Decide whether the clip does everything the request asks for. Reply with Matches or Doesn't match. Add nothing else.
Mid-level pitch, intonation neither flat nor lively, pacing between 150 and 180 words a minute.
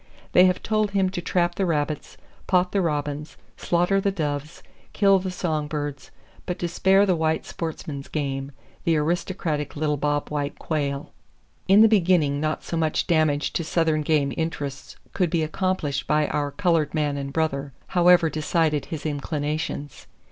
Matches